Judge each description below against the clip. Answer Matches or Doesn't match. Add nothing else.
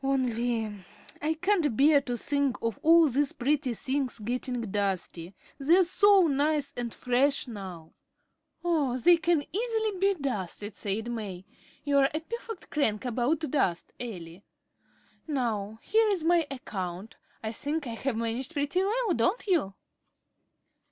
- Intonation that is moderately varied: Doesn't match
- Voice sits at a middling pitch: Doesn't match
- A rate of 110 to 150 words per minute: Matches